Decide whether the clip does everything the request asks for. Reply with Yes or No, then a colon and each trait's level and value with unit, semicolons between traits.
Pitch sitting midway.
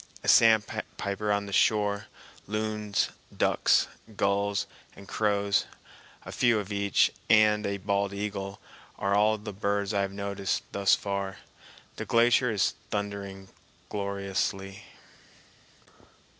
No: low, 100 Hz